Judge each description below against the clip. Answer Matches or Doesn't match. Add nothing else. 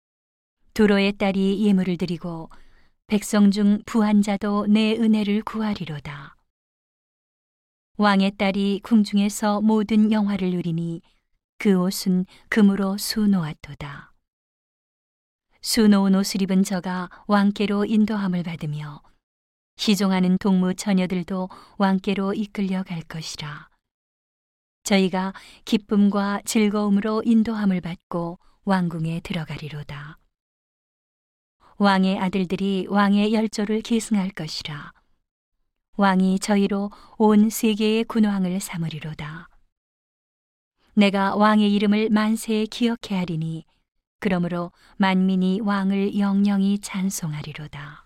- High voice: Matches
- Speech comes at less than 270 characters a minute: Matches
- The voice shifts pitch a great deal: Doesn't match